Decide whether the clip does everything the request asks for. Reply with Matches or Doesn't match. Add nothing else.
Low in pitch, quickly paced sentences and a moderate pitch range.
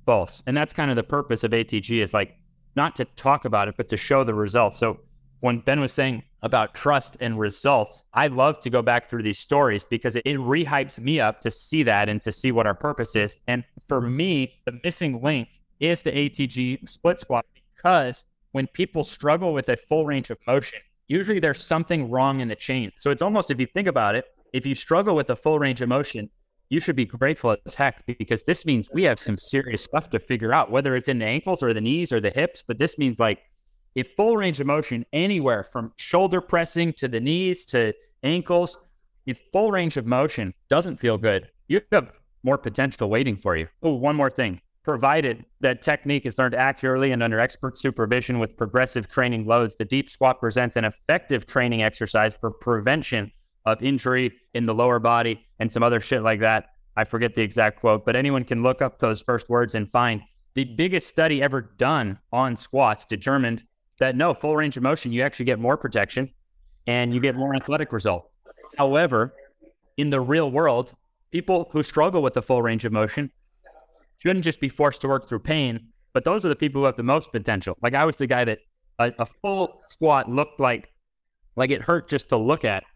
Matches